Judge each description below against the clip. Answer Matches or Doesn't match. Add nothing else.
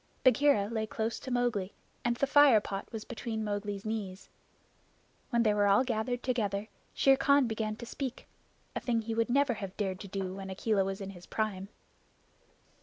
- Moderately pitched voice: Doesn't match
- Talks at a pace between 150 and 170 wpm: Doesn't match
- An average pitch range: Matches